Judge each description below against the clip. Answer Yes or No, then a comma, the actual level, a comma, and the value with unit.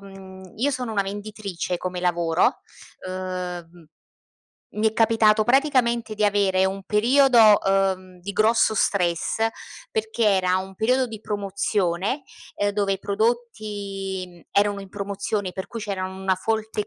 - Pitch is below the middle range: No, high, 200 Hz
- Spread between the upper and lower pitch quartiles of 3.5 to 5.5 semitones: No, narrow, 2.6 semitones